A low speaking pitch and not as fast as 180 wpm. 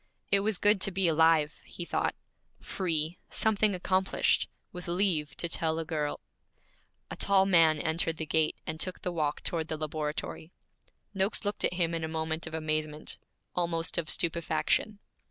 No: medium, 165 Hz; average, 165 wpm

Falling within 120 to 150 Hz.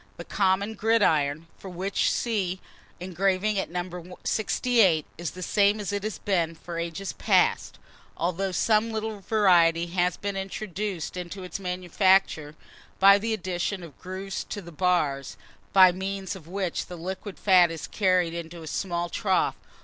No: medium, 185 Hz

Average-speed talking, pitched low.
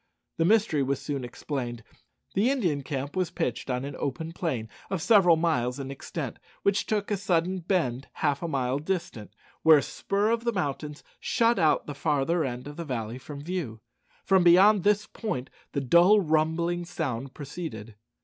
No: average, 175 wpm; medium, 160 Hz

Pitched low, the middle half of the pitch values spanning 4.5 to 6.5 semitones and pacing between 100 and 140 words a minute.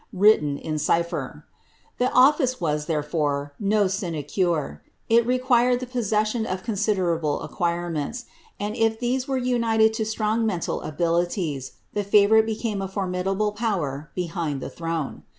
No: high, 200 Hz; average, 5.2 semitones; slow, 135 wpm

